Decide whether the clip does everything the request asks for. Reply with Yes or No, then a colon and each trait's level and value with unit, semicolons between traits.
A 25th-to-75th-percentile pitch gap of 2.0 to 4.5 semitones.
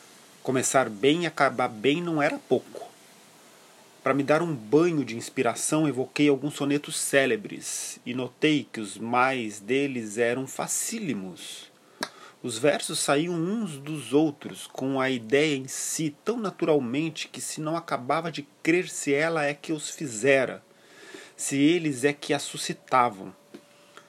Yes: average, 3.1 semitones